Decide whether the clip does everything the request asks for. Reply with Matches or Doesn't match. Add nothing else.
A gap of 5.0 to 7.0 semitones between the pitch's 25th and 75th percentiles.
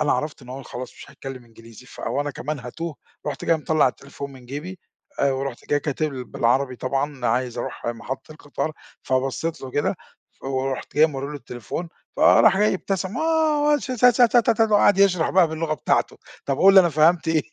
Matches